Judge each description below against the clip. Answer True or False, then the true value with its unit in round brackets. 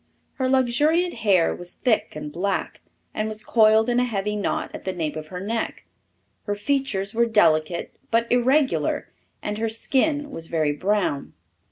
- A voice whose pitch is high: True (215 Hz)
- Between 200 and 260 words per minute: False (165 wpm)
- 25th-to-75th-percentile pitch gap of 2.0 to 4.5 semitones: False (5.1 semitones)